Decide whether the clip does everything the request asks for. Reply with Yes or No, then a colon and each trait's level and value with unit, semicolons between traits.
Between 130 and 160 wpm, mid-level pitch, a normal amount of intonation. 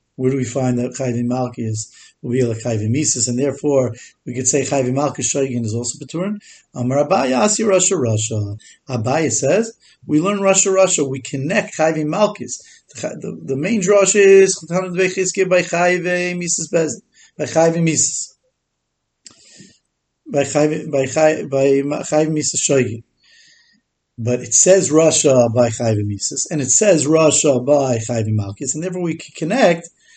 No: slow, 135 wpm; medium, 150 Hz; wide, 6.1 semitones